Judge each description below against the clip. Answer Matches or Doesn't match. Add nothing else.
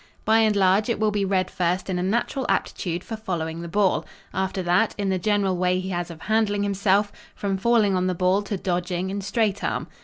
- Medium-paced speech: Doesn't match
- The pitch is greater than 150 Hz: Matches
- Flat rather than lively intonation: Matches